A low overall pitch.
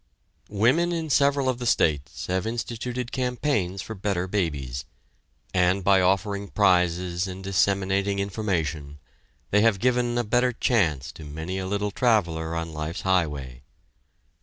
Yes: very low, 95 Hz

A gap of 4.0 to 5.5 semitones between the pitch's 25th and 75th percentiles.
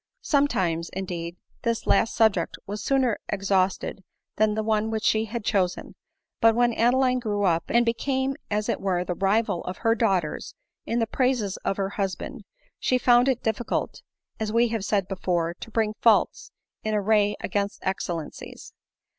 No: average, 3.3 semitones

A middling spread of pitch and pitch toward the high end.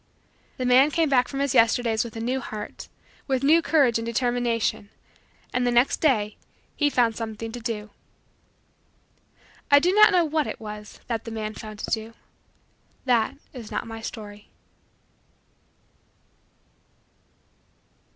Yes: average, 3.5 semitones; high, 235 Hz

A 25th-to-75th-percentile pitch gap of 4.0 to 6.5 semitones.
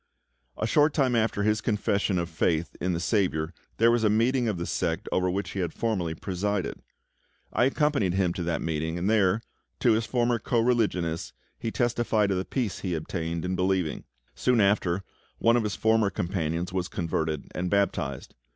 Yes: average, 4.6 semitones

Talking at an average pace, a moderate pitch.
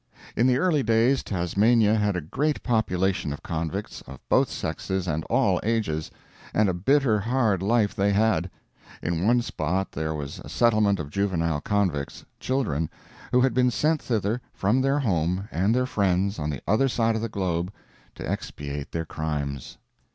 No: average, 170 wpm; low, 100 Hz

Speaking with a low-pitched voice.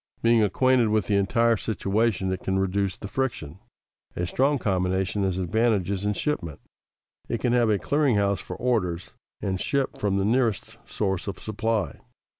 Yes: low, 105 Hz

